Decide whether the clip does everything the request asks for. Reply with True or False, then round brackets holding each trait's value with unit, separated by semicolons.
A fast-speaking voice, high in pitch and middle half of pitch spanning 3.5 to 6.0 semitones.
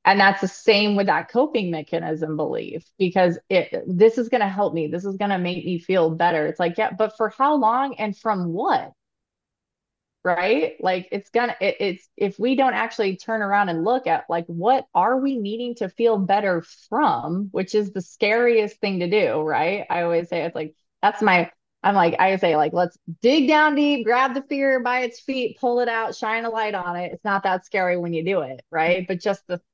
True (220 wpm; 200 Hz; 4.5 semitones)